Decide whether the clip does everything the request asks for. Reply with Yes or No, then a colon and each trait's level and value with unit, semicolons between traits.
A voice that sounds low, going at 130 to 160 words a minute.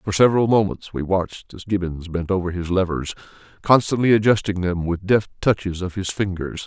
No: very low, 95 Hz; average, 180 wpm